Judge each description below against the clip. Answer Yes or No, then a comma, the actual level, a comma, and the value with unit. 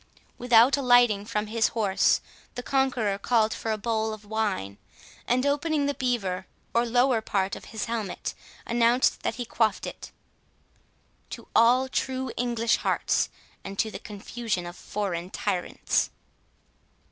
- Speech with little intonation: No, average, 3.2 semitones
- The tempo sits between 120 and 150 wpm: Yes, average, 140 wpm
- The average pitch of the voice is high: Yes, high, 230 Hz